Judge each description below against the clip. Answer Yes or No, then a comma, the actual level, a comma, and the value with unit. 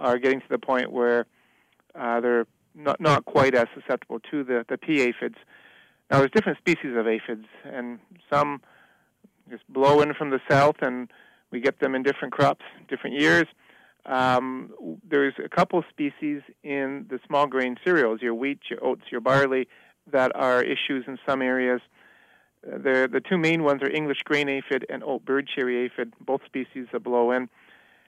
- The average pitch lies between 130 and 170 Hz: Yes, low, 135 Hz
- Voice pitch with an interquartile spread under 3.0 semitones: Yes, narrow, 2.5 semitones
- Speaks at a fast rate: No, average, 175 wpm